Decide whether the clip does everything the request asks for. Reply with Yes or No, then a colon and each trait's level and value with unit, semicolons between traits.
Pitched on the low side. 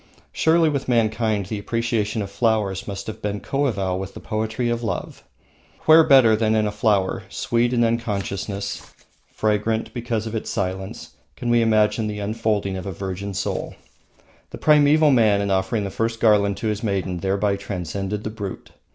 Yes: low, 105 Hz